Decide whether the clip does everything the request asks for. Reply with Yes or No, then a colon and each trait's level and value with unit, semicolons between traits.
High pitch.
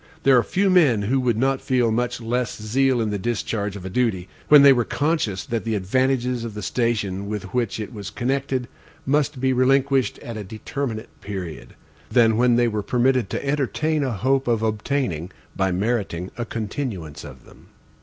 No: low, 120 Hz